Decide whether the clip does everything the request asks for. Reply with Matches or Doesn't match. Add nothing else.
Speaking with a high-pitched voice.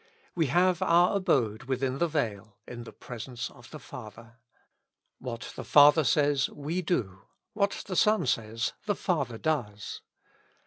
Doesn't match